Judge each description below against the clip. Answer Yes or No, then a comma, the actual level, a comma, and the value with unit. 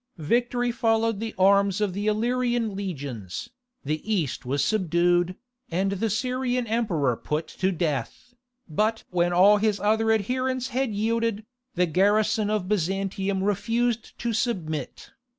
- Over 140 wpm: No, slow, 135 wpm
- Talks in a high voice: Yes, high, 205 Hz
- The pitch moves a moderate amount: Yes, average, 4.2 semitones